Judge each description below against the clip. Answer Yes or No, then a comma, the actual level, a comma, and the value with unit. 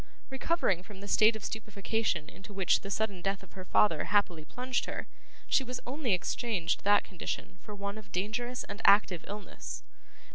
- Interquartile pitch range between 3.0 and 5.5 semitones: No, narrow, 2.6 semitones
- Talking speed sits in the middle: Yes, average, 170 wpm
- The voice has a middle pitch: No, high, 200 Hz